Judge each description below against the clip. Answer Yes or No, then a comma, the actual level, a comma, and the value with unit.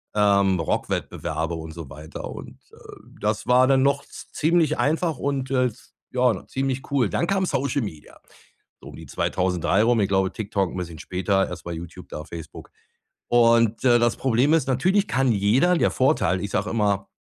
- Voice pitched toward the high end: No, low, 115 Hz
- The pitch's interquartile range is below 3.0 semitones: No, wide, 6.2 semitones